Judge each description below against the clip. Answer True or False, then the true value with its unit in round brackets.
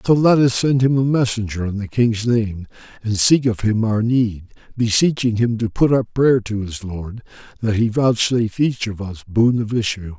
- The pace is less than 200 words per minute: False (205 wpm)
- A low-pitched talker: True (115 Hz)